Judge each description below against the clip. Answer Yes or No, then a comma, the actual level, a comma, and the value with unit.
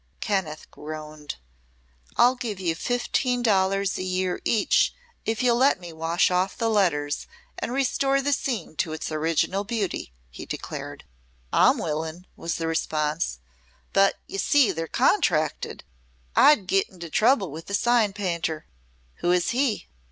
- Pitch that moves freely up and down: Yes, wide, 6.0 semitones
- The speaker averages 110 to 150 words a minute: Yes, average, 145 wpm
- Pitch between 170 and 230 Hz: Yes, high, 190 Hz